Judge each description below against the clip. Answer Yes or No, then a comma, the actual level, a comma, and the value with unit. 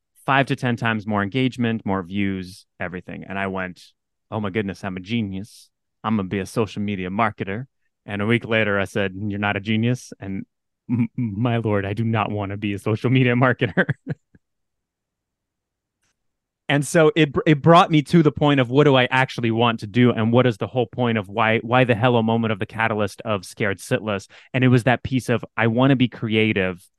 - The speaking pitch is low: Yes, low, 115 Hz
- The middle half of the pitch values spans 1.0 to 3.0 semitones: No, average, 3.7 semitones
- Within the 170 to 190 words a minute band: No, fast, 205 wpm